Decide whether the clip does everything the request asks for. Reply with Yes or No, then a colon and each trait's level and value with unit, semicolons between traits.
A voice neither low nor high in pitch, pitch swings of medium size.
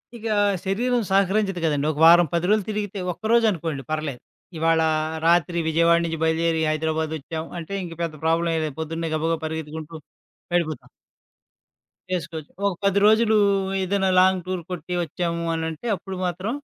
Yes: medium, 170 Hz; average, 3.1 semitones